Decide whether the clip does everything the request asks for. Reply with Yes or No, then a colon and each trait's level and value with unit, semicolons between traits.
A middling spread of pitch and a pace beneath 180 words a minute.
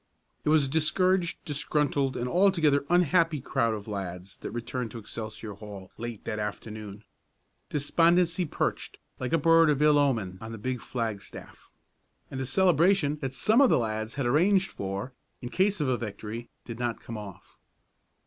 No: wide, 6.7 semitones; average, 170 wpm